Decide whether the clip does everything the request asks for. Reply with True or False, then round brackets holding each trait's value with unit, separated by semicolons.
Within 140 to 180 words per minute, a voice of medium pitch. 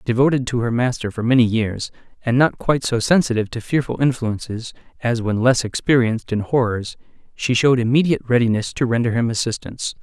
False (175 wpm; 120 Hz)